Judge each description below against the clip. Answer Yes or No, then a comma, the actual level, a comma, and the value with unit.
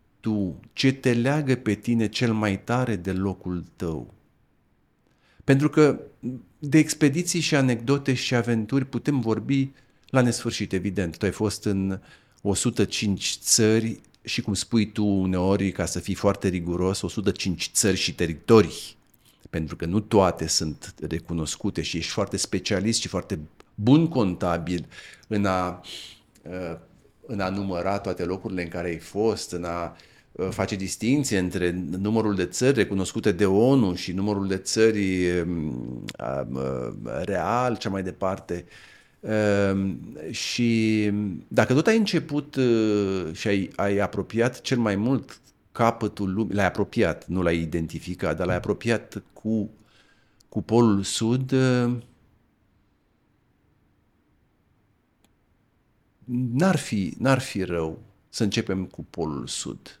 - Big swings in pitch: No, average, 4.2 semitones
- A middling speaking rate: Yes, average, 125 wpm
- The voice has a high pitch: No, low, 100 Hz